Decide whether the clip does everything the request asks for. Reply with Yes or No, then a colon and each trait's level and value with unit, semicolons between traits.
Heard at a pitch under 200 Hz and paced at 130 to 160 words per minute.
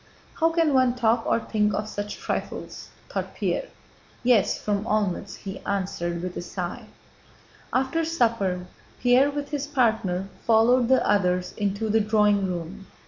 No: high, 215 Hz; average, 145 wpm